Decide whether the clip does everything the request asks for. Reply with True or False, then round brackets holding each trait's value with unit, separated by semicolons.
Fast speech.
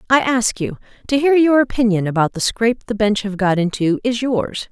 True (215 wpm)